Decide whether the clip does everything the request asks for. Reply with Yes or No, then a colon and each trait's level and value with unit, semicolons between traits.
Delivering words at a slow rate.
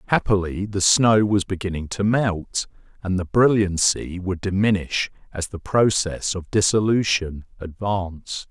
Yes: slow, 125 wpm